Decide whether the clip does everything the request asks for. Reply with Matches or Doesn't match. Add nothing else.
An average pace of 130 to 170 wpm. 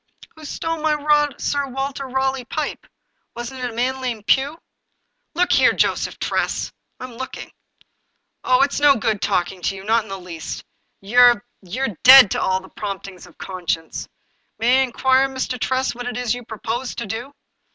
Doesn't match